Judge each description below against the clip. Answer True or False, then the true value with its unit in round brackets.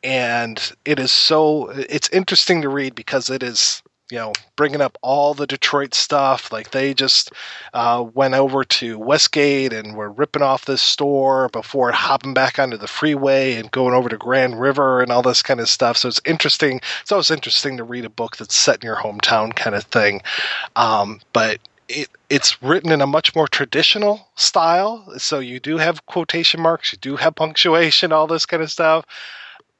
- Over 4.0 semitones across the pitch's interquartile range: False (3.7 semitones)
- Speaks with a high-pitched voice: False (135 Hz)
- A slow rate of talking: False (190 wpm)